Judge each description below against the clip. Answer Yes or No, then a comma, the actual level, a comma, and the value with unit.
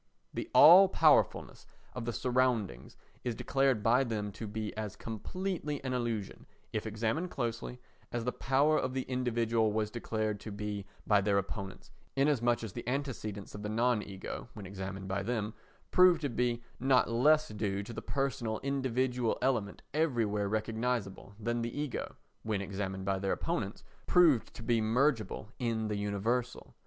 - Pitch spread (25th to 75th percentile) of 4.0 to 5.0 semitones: No, average, 3.6 semitones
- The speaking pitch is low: Yes, low, 115 Hz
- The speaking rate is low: No, average, 160 wpm